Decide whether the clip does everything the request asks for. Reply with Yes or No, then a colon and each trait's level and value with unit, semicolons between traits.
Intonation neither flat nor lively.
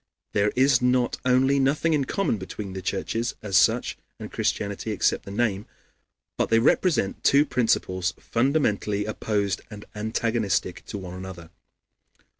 Yes: average, 4.4 semitones